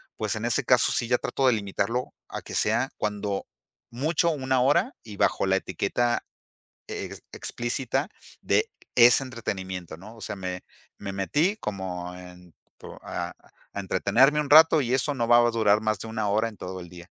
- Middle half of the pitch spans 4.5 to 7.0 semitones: Yes, average, 5.1 semitones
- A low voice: Yes, low, 110 Hz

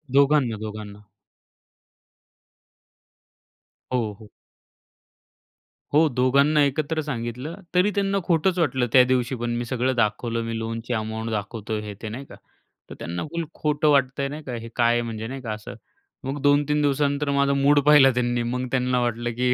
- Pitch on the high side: No, low, 125 Hz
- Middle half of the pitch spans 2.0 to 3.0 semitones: No, average, 3.7 semitones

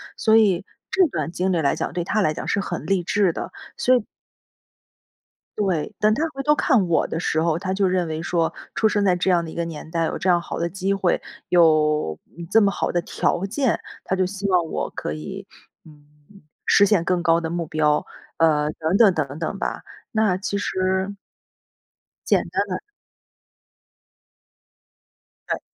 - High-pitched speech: No, medium, 180 Hz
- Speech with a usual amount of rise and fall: Yes, average, 3.5 semitones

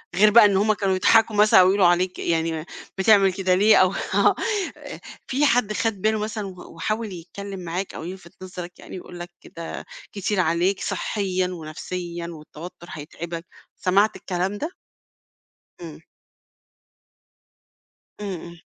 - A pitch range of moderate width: Yes, average, 3.1 semitones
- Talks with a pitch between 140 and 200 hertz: Yes, medium, 185 Hz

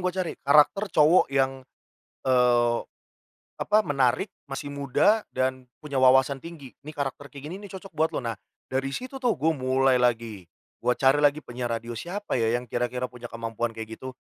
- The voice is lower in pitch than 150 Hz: Yes, low, 135 Hz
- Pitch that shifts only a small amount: No, average, 3.6 semitones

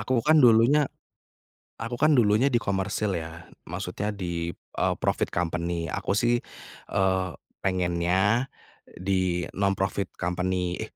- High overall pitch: No, very low, 95 Hz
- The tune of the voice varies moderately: Yes, average, 4.4 semitones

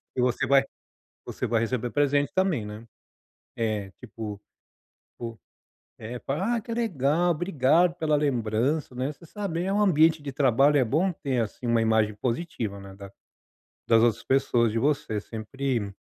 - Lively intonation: Yes, wide, 5.7 semitones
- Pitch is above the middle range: No, low, 130 Hz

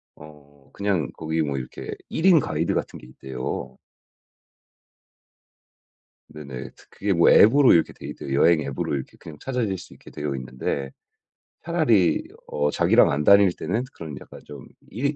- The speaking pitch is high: No, very low, 75 Hz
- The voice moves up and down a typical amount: No, wide, 6.4 semitones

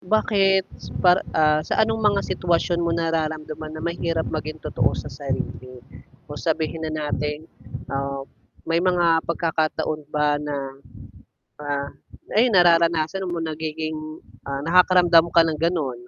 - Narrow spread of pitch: Yes, narrow, 2.3 semitones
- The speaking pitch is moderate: Yes, medium, 160 Hz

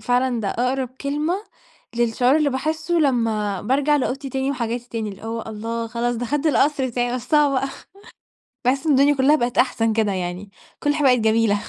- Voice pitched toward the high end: Yes, very high, 250 Hz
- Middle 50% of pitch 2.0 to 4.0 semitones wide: Yes, average, 3.6 semitones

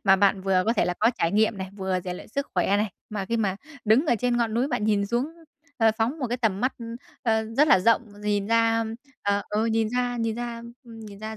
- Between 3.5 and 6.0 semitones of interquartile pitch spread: No, average, 2.7 semitones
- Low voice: No, high, 220 Hz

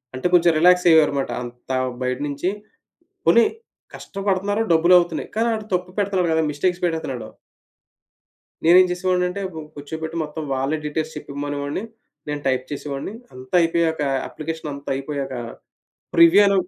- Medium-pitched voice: Yes, medium, 160 Hz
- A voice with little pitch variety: No, average, 3.9 semitones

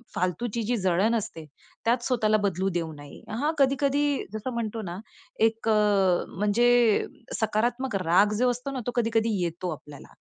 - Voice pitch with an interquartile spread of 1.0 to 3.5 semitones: No, average, 4.2 semitones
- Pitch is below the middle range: No, high, 220 Hz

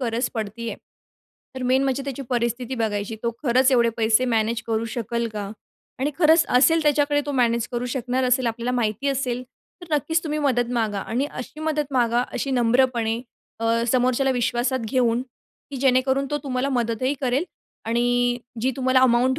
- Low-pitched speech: No, very high, 250 Hz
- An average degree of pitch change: No, narrow, 2.3 semitones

